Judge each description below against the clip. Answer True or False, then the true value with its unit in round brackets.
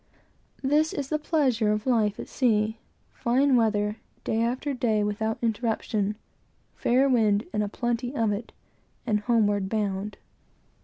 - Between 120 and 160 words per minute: True (140 wpm)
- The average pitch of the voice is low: False (225 Hz)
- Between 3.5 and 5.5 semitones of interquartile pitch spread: False (3.0 semitones)